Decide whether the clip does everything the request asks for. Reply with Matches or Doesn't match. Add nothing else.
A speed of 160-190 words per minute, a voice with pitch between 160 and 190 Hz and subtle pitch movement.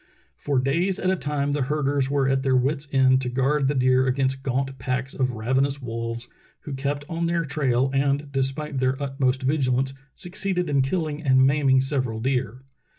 Doesn't match